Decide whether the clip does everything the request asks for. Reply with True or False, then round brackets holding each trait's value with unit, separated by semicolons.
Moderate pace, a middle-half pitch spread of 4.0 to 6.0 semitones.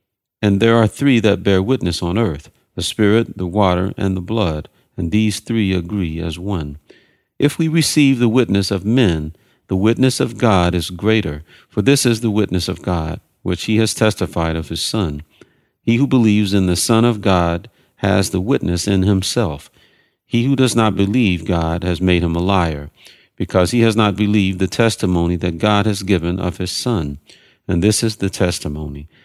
True (190 wpm; 4.3 semitones)